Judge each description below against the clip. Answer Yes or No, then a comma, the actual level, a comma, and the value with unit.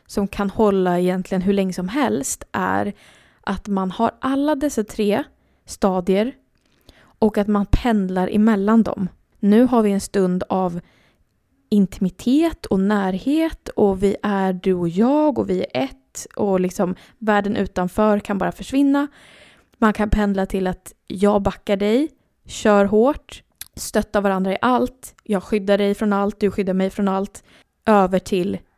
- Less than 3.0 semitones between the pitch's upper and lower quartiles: Yes, narrow, 2.4 semitones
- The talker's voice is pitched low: No, high, 200 Hz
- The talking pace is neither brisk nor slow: Yes, average, 155 wpm